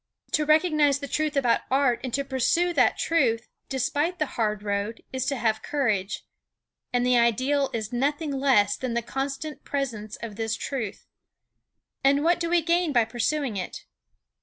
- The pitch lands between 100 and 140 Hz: No, very high, 265 Hz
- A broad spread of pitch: No, average, 4.3 semitones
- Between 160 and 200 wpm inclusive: Yes, average, 165 wpm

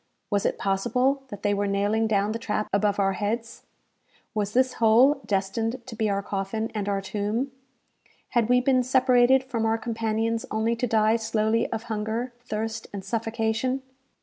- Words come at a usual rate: Yes, average, 170 wpm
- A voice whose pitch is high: Yes, high, 225 Hz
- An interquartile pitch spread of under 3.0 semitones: Yes, narrow, 2.5 semitones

